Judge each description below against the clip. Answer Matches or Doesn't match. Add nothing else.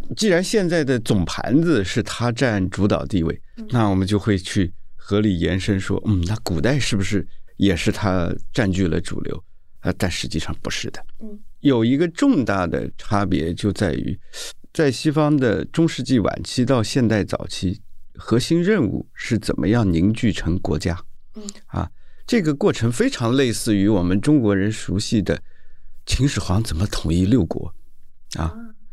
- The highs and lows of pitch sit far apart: Matches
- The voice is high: Doesn't match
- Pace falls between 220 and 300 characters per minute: Matches